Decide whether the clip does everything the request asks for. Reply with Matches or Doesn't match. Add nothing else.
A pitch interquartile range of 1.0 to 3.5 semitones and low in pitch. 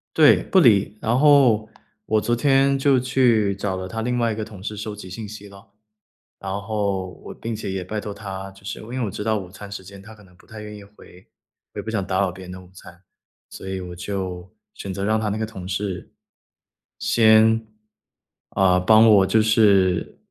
Matches